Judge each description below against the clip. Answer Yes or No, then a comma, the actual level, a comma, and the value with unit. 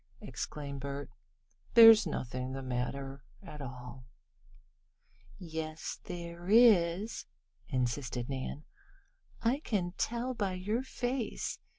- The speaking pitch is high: No, medium, 160 Hz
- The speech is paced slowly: Yes, slow, 95 wpm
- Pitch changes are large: Yes, wide, 7.9 semitones